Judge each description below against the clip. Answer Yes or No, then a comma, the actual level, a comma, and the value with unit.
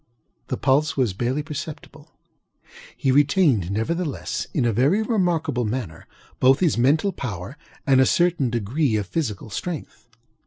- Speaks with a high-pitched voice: No, low, 135 Hz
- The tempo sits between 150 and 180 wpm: No, average, 140 wpm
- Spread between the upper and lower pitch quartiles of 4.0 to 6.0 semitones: Yes, average, 5.3 semitones